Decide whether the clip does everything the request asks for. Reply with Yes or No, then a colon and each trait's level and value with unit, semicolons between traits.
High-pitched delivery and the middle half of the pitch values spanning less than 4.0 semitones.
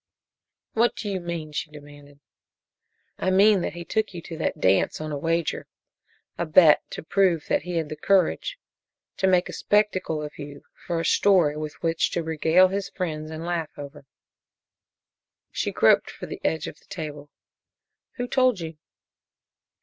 No: medium, 165 Hz; average, 3.6 semitones